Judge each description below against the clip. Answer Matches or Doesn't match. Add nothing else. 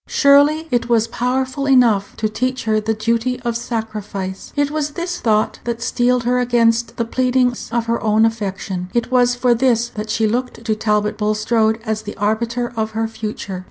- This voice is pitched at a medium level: Doesn't match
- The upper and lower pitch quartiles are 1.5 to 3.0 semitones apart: Matches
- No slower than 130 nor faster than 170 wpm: Doesn't match